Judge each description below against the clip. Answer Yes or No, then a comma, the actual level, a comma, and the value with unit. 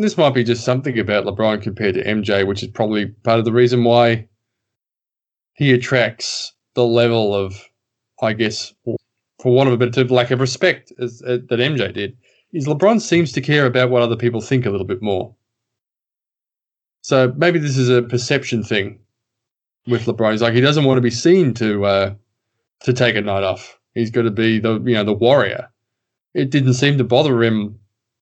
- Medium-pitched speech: No, low, 120 Hz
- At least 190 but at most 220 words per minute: Yes, average, 200 wpm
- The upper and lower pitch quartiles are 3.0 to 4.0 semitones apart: No, narrow, 2.4 semitones